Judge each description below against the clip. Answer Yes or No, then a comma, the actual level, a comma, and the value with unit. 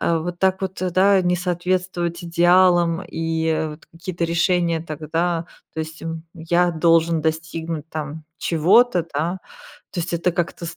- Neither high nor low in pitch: Yes, medium, 170 Hz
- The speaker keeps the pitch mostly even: Yes, narrow, 1.6 semitones